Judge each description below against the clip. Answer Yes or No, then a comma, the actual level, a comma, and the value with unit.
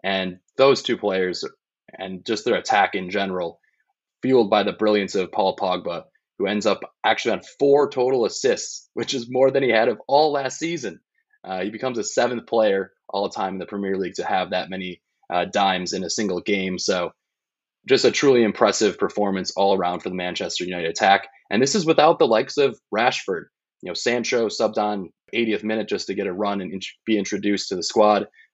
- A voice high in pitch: No, low, 105 Hz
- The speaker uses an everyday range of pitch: No, wide, 5.9 semitones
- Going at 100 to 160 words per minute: No, fast, 205 wpm